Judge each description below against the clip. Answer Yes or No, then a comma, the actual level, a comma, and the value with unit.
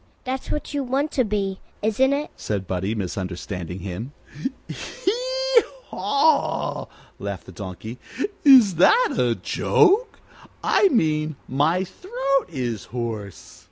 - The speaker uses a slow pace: Yes, slow, 120 wpm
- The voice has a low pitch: No, high, 190 Hz